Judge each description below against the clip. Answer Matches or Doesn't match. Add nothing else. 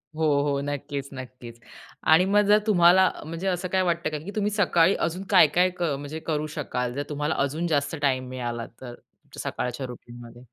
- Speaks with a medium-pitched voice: Matches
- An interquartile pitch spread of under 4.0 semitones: Doesn't match